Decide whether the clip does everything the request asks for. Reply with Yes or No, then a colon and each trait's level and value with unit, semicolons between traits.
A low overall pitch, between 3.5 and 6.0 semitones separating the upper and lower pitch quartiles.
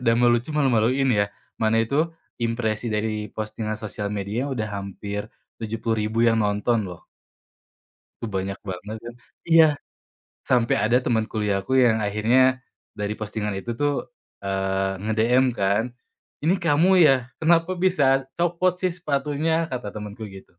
Yes: low, 110 Hz; average, 3.9 semitones